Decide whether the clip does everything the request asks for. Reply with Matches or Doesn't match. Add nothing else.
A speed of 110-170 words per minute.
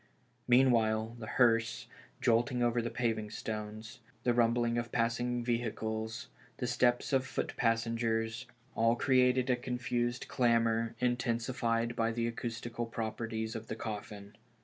Matches